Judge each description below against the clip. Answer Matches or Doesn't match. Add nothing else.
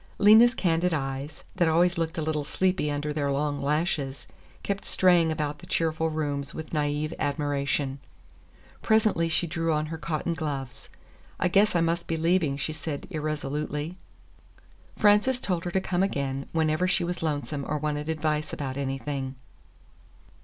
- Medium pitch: Matches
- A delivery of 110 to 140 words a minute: Doesn't match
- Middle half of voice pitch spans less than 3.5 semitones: Matches